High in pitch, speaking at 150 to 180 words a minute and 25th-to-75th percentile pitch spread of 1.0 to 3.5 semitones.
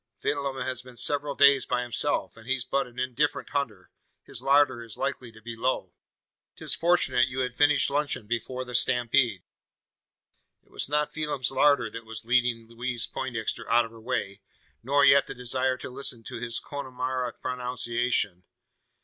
No: low, 125 Hz; average, 170 wpm; average, 2.8 semitones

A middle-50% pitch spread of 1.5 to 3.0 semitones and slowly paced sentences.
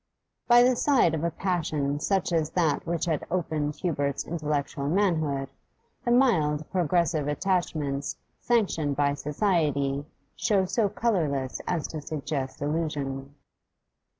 No: average, 4.2 semitones; slow, 125 wpm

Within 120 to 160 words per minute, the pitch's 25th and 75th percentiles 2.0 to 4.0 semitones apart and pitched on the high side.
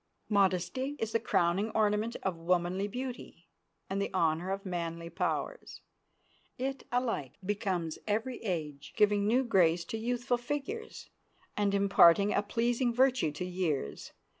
No: slow, 135 wpm; average, 5.3 semitones; high, 200 Hz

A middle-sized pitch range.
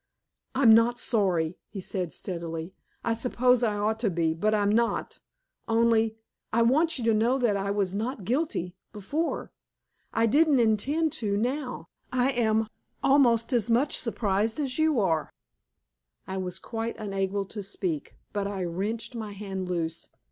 Yes: average, 3.9 semitones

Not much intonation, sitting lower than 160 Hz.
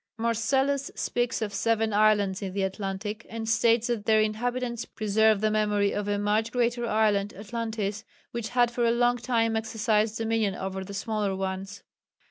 No: narrow, 2.2 semitones; high, 220 Hz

